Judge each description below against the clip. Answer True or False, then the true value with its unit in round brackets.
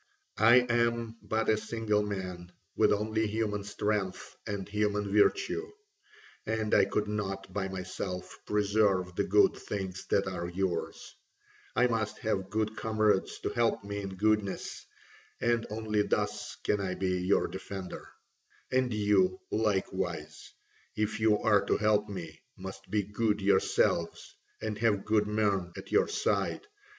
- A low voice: True (105 Hz)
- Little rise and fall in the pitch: True (2.2 semitones)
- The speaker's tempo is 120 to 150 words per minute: True (140 wpm)